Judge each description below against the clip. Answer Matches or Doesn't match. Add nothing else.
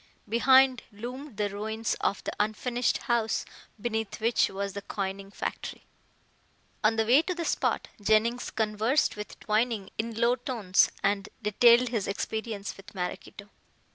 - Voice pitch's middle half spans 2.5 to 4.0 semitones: Matches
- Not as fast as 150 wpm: Matches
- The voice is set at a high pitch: Matches